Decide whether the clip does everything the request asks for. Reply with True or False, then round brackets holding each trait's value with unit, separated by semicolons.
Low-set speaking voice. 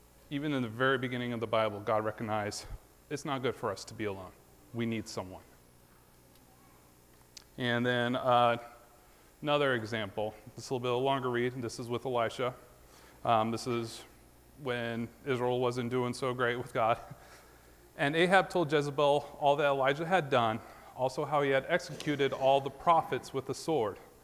True (120 Hz)